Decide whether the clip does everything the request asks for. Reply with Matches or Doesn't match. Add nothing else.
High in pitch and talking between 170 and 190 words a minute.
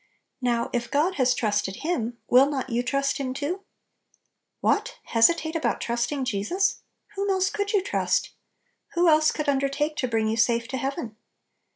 Matches